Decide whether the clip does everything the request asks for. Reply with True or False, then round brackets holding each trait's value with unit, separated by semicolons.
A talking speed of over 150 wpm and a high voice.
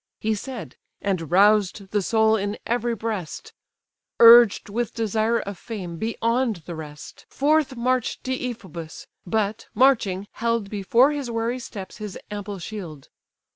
False (135 wpm; 220 Hz)